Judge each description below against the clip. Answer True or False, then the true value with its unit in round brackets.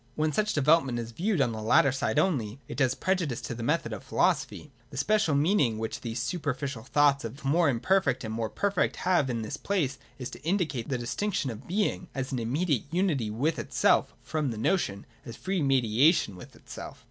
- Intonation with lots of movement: True (6.1 semitones)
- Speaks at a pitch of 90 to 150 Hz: True (140 Hz)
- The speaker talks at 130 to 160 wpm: False (200 wpm)